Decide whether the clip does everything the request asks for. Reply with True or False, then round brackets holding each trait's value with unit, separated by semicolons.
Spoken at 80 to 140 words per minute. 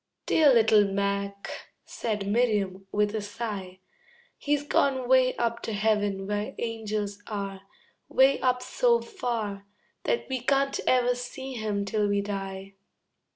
True (135 wpm)